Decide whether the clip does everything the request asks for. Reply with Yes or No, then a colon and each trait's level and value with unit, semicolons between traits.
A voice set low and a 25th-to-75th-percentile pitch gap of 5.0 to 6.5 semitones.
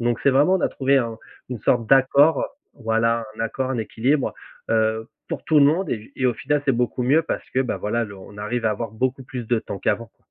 No: low, 120 Hz; average, 3.2 semitones